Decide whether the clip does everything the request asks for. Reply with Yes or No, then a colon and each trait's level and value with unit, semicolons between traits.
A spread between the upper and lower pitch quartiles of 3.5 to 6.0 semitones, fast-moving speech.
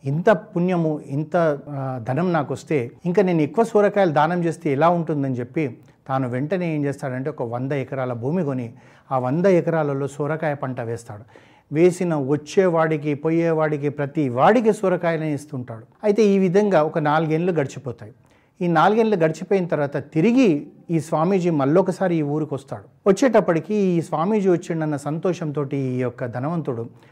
Yes: average, 4.2 semitones; fast, 135 wpm